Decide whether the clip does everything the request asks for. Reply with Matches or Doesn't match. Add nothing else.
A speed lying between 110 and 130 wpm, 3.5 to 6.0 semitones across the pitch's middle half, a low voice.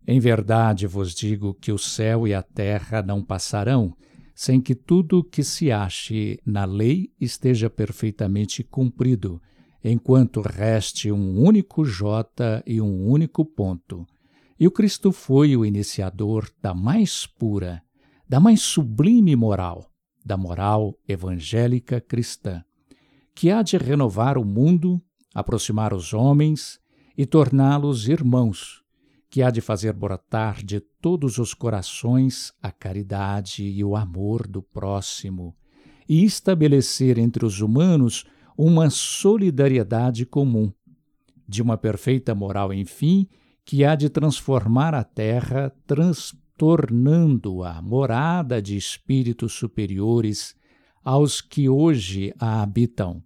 Matches